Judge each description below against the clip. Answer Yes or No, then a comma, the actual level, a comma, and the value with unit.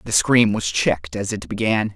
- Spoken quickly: Yes, fast, 215 wpm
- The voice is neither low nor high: No, low, 100 Hz